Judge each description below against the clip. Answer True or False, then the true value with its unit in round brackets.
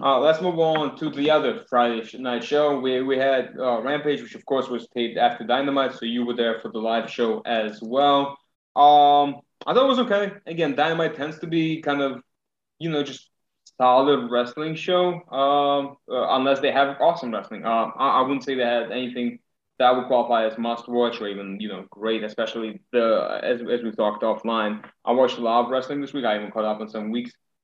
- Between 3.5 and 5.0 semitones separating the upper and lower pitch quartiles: True (3.8 semitones)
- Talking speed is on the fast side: True (215 wpm)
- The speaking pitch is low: True (130 Hz)